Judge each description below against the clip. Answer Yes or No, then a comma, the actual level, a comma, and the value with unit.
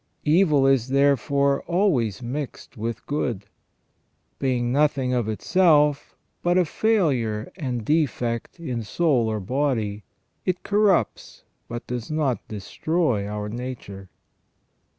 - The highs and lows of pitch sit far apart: No, average, 4.8 semitones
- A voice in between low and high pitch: No, low, 130 Hz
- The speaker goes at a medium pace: No, slow, 115 wpm